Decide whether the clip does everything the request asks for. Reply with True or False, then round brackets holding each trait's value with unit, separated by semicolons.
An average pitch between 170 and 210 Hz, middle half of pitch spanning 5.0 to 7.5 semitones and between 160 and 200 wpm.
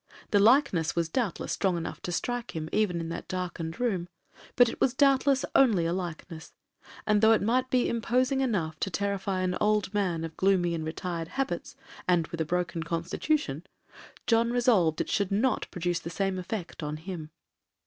True (185 Hz; 5.4 semitones; 180 wpm)